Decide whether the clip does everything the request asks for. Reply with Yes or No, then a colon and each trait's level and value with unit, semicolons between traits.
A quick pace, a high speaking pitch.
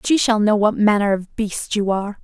Yes: fast, 240 wpm; high, 210 Hz